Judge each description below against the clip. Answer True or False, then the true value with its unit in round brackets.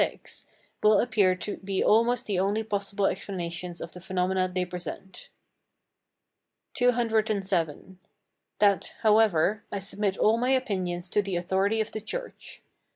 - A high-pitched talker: True (200 Hz)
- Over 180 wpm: False (135 wpm)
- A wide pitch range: False (2.9 semitones)